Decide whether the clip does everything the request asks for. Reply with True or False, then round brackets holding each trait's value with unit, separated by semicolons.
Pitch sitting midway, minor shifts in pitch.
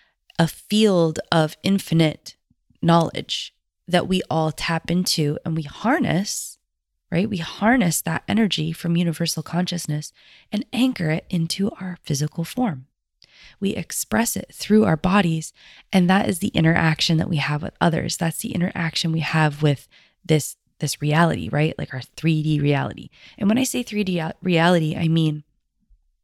False (165 Hz; 3.2 semitones)